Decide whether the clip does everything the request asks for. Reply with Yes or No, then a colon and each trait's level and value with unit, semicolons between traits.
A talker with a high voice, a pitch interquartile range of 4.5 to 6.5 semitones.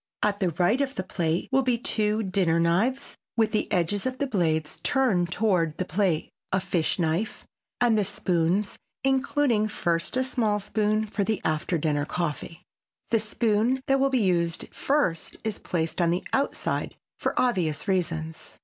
Yes: high, 200 Hz; average, 5.2 semitones